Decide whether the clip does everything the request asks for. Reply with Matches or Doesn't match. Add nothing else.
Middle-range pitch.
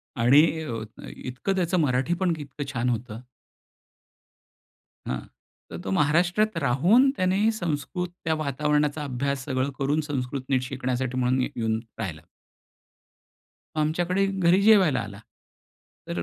Matches